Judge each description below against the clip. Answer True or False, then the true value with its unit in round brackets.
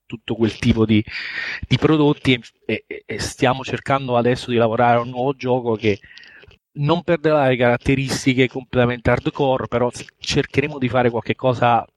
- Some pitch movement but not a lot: False (2.3 semitones)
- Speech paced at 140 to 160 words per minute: True (155 wpm)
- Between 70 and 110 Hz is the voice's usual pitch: False (125 Hz)